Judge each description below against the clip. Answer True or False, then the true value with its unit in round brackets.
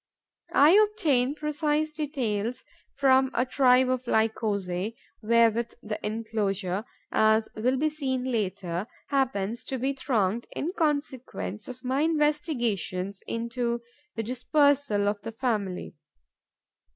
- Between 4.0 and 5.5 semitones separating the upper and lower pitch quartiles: True (4.5 semitones)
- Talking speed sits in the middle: False (115 wpm)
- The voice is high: True (240 Hz)